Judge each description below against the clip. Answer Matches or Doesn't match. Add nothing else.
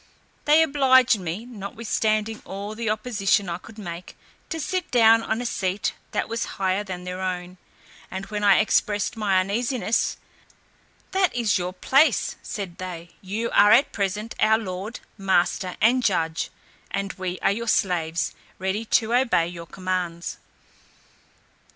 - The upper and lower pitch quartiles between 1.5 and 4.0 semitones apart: Matches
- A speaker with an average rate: Matches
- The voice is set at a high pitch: Matches